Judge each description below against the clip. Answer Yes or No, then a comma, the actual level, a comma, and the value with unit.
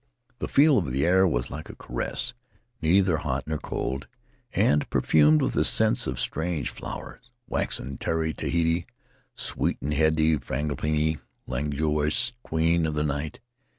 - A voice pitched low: Yes, very low, 80 Hz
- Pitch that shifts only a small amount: Yes, narrow, 2.0 semitones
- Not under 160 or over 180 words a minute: No, average, 150 wpm